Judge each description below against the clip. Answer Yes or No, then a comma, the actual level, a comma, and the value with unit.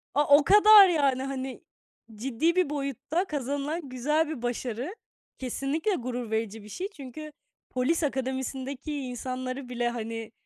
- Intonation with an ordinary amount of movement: Yes, average, 3.7 semitones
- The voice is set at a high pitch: Yes, very high, 270 Hz